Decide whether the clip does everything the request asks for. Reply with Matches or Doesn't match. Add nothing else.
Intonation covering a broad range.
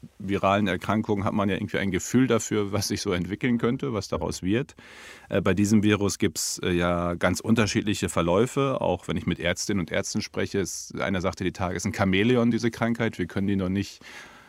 Doesn't match